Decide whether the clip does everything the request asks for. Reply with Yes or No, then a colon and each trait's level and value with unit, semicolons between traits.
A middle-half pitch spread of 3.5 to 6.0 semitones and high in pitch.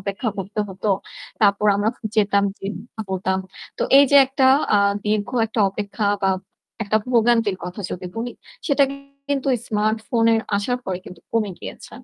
No: narrow, 2.4 semitones; high, 215 Hz